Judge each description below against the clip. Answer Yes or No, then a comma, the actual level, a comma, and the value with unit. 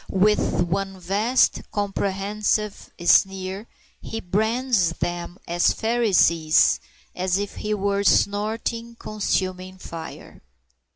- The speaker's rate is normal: No, slow, 95 wpm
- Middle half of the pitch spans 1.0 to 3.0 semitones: Yes, narrow, 2.4 semitones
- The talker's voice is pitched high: Yes, high, 200 Hz